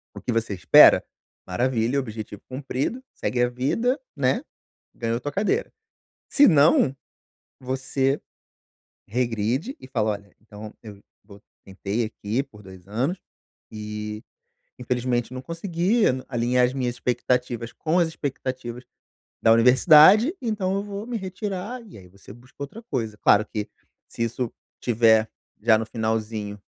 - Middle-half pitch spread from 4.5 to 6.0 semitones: Yes, average, 5.3 semitones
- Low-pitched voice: Yes, low, 125 Hz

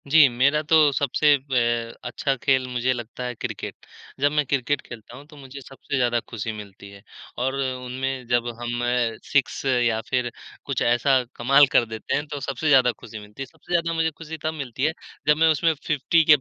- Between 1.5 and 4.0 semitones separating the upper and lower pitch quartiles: Yes, average, 3.2 semitones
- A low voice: Yes, low, 130 Hz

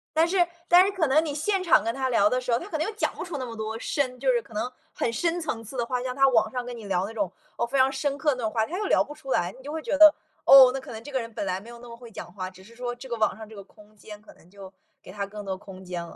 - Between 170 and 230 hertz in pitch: No, high, 245 Hz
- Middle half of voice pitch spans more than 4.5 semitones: Yes, average, 4.9 semitones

